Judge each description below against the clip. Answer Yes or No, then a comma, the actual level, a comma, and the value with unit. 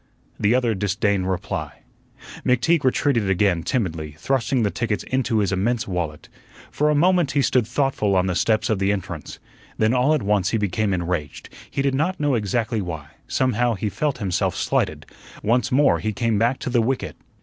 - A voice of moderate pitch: No, low, 110 Hz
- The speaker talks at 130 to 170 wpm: No, average, 185 wpm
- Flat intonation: No, average, 5.0 semitones